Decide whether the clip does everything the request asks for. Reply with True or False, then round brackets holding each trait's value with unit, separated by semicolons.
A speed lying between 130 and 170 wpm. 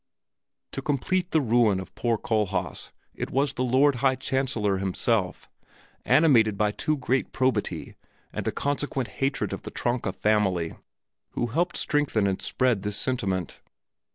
True (145 wpm)